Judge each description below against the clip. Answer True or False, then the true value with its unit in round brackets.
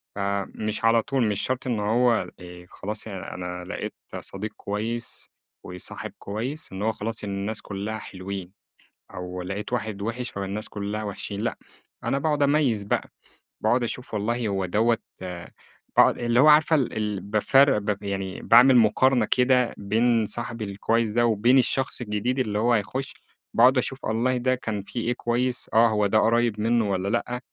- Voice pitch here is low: True (110 Hz)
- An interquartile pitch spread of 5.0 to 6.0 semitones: False (3.2 semitones)